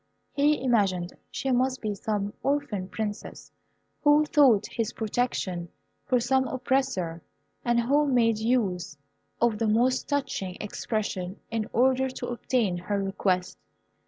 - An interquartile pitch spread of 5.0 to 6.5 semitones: No, average, 4.6 semitones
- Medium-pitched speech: No, high, 230 Hz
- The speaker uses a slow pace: Yes, slow, 130 wpm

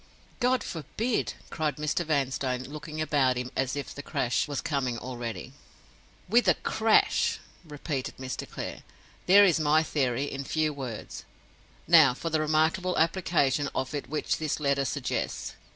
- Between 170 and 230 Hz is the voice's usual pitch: No, medium, 150 Hz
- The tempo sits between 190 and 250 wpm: No, average, 150 wpm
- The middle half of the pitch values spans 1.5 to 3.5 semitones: Yes, average, 3.1 semitones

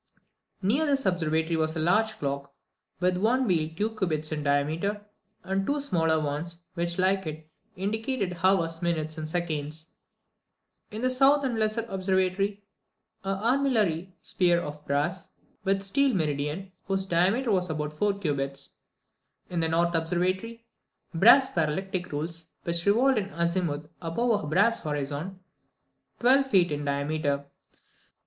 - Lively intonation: No, average, 4.6 semitones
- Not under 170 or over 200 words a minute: No, average, 145 wpm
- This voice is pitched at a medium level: Yes, medium, 180 Hz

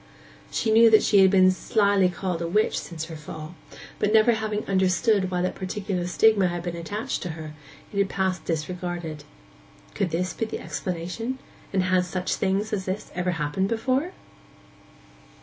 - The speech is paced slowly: No, average, 170 wpm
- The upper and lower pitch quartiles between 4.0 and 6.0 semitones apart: No, average, 3.2 semitones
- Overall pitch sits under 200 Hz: Yes, medium, 185 Hz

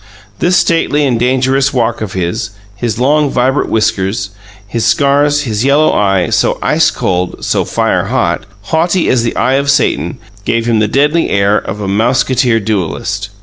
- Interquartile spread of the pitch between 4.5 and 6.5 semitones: Yes, average, 5.1 semitones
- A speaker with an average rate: Yes, average, 165 wpm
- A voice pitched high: No, low, 120 Hz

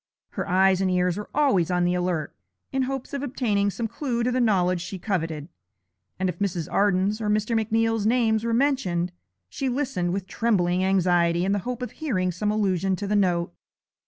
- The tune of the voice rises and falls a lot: No, average, 4.3 semitones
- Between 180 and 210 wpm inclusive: Yes, average, 190 wpm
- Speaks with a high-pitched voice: Yes, high, 200 Hz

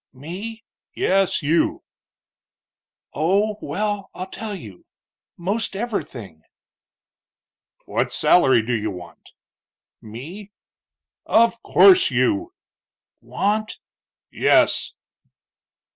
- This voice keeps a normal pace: No, slow, 80 wpm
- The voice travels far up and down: Yes, wide, 8.3 semitones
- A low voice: No, high, 195 Hz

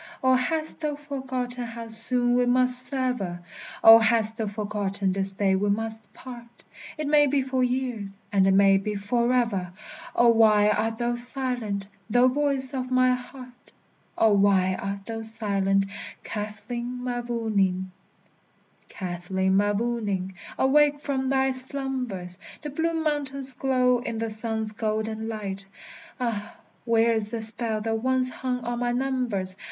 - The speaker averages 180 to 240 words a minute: No, average, 145 wpm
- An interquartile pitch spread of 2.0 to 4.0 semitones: Yes, average, 3.6 semitones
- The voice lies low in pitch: No, high, 230 Hz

